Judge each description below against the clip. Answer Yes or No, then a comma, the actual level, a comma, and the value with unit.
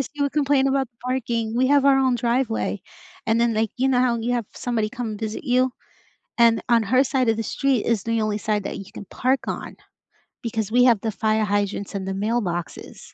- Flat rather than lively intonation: No, average, 3.0 semitones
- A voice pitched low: No, high, 235 Hz